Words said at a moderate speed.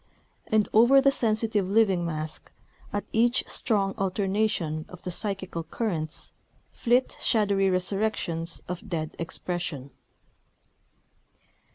No: slow, 100 wpm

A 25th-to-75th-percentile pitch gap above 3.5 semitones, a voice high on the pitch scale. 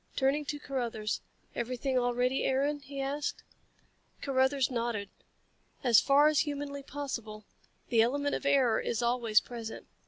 No: average, 3.1 semitones; very high, 265 Hz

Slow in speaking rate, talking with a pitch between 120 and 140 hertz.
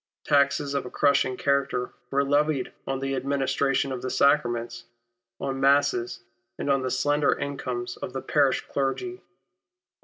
No: average, 145 wpm; low, 135 Hz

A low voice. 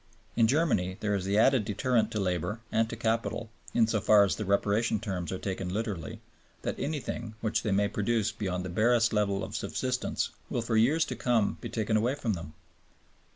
Yes: low, 110 Hz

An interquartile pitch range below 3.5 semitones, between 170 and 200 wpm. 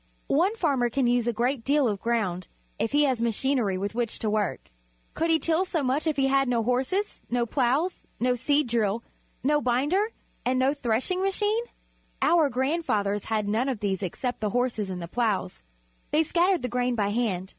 No: average, 4.8 semitones; average, 195 wpm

